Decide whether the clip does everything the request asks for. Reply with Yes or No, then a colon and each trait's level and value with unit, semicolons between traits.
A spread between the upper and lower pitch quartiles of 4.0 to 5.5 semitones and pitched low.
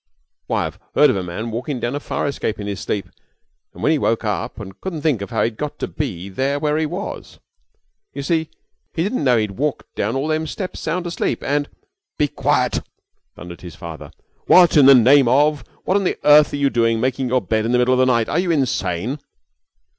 Yes: average, 5.1 semitones; low, 130 Hz